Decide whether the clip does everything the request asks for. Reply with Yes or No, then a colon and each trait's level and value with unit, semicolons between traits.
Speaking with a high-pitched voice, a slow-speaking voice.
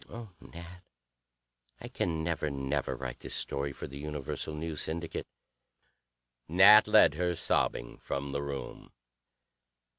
No: very low, 75 Hz; slow, 125 wpm